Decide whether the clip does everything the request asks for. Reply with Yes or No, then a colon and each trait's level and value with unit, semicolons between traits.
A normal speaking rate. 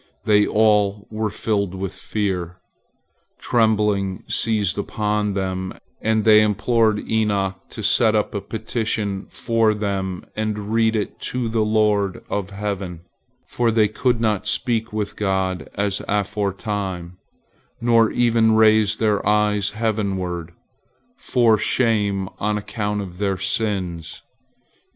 No: slow, 125 wpm